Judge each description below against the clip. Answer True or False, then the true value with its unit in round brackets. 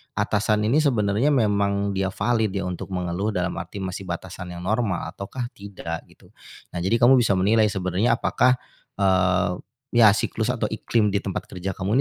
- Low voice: True (100 Hz)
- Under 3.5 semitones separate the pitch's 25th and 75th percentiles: True (2.9 semitones)